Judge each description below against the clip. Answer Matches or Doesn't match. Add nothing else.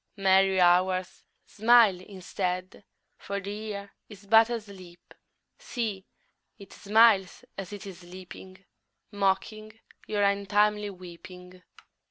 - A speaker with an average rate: Doesn't match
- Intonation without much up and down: Matches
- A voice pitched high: Matches